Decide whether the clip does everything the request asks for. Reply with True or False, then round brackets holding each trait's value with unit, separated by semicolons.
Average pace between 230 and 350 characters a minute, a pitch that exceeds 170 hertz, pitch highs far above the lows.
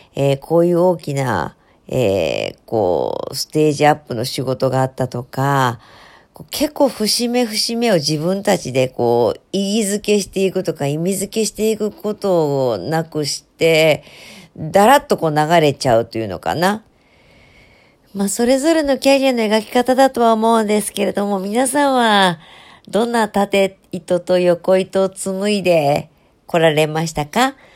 True (290 characters per minute; 190 Hz; 6.0 semitones)